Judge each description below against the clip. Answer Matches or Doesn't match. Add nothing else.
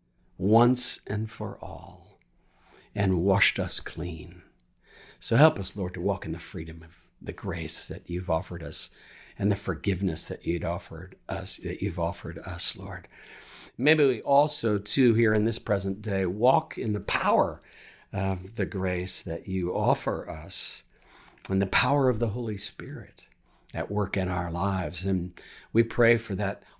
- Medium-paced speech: Matches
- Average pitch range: Matches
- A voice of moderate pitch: Doesn't match